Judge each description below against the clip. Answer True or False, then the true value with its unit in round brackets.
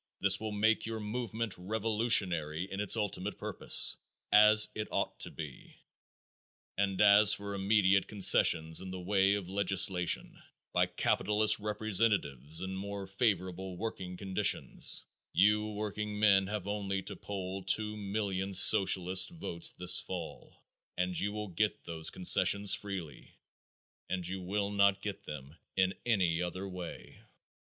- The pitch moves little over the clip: True (2.3 semitones)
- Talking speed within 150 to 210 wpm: False (135 wpm)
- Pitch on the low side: True (100 Hz)